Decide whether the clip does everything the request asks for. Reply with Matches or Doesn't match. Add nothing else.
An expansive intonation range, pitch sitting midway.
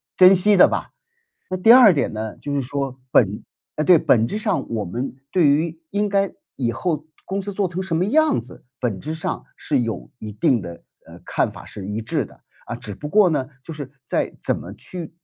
Matches